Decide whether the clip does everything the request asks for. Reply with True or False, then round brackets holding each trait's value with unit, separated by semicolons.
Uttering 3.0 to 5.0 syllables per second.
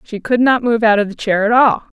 False (5.5 syllables/s)